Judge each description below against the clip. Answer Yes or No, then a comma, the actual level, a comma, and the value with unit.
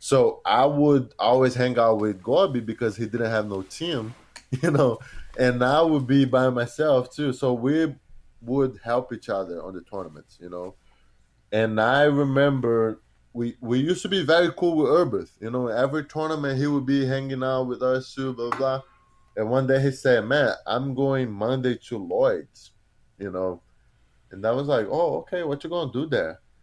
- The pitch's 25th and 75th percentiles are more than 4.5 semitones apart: No, average, 3.6 semitones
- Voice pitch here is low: Yes, low, 130 Hz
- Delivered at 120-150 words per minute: No, average, 190 wpm